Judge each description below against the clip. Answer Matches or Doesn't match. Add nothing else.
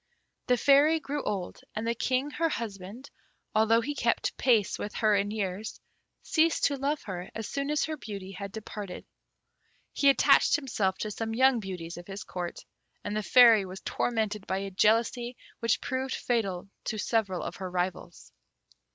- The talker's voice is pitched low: Doesn't match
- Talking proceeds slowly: Doesn't match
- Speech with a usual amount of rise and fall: Matches